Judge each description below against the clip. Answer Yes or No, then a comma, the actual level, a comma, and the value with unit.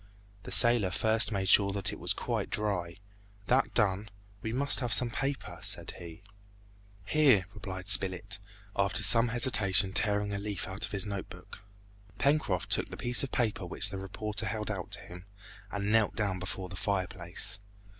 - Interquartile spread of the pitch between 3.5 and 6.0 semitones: No, average, 3.0 semitones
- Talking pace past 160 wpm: Yes, average, 175 wpm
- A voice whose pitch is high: No, low, 100 Hz